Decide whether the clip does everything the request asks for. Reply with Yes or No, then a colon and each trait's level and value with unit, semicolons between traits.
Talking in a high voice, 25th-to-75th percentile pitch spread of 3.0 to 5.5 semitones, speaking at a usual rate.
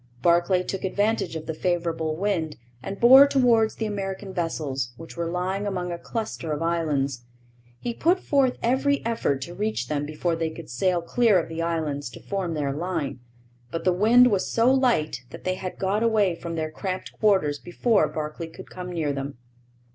No: medium, 180 Hz; average, 4.7 semitones; average, 185 wpm